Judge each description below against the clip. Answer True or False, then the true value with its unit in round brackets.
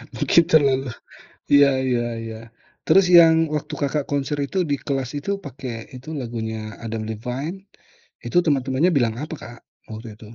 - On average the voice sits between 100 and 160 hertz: True (135 Hz)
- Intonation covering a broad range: False (3.6 semitones)